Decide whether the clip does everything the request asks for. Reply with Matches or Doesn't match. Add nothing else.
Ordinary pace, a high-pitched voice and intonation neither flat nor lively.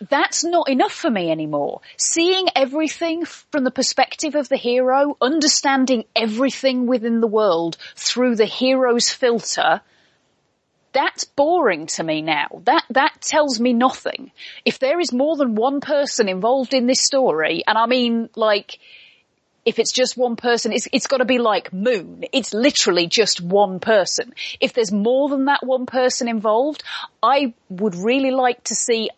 Matches